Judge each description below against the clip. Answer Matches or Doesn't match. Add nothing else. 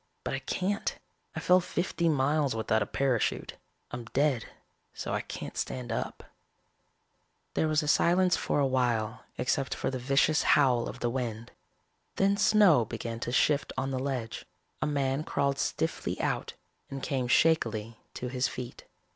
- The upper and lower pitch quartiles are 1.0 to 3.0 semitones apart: Doesn't match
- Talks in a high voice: Doesn't match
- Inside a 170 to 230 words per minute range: Doesn't match